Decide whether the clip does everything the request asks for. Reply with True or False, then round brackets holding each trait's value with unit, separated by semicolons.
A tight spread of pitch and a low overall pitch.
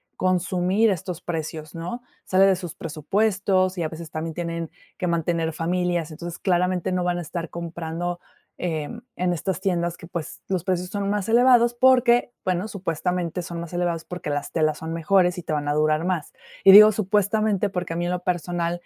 False (2.3 semitones; 175 Hz)